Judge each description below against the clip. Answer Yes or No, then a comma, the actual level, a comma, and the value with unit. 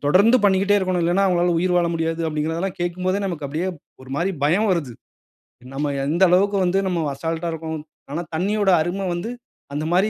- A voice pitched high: No, medium, 175 Hz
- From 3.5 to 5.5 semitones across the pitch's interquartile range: No, average, 2.8 semitones